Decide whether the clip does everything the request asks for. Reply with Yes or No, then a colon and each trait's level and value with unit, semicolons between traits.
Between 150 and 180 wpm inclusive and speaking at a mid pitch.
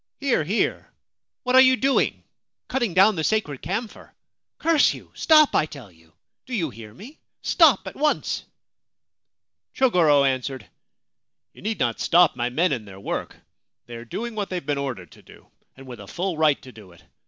No: average, 195 wpm; medium, 165 Hz